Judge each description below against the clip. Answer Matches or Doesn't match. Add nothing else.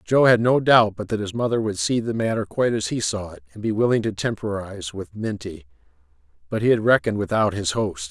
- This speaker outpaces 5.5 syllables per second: Matches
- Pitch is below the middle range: Matches